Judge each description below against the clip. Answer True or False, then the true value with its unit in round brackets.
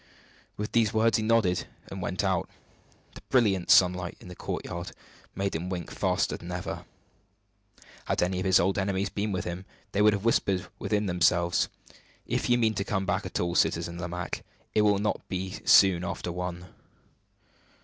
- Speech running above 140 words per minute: True (175 wpm)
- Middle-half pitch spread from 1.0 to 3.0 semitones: True (2.7 semitones)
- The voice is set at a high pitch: False (95 Hz)